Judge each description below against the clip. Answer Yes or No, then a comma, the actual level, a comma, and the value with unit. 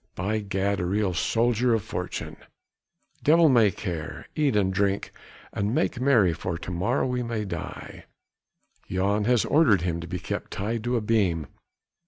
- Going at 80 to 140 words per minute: No, average, 165 wpm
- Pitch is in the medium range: No, low, 105 Hz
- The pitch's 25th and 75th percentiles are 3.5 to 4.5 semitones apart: Yes, average, 4.2 semitones